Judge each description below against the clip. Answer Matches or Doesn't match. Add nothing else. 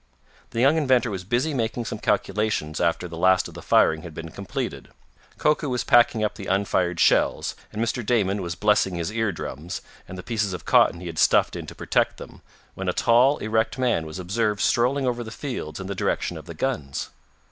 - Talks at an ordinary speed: Doesn't match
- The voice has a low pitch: Matches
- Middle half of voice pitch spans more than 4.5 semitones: Matches